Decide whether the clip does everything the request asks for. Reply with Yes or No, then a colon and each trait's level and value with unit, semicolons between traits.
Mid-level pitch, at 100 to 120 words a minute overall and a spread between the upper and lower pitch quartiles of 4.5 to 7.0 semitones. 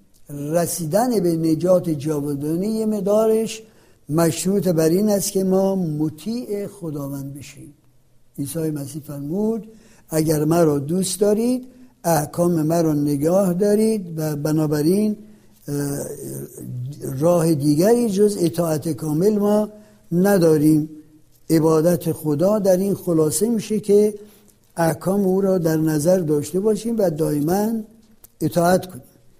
Yes: medium, 170 Hz; slow, 105 wpm; average, 5.0 semitones